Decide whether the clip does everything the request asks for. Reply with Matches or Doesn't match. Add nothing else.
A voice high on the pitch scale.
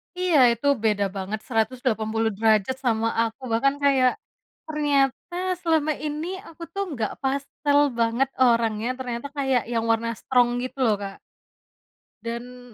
Matches